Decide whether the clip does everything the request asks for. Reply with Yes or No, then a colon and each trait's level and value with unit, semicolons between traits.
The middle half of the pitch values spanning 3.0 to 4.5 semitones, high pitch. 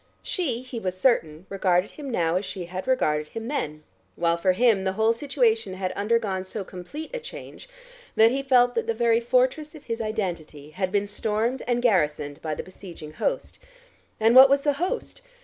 No: wide, 5.4 semitones; high, 220 Hz